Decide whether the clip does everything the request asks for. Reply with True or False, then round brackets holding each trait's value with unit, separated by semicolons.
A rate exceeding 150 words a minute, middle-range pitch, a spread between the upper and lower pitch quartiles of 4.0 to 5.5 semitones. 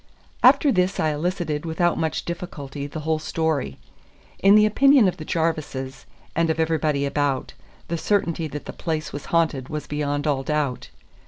False (165 wpm; 155 Hz; 2.8 semitones)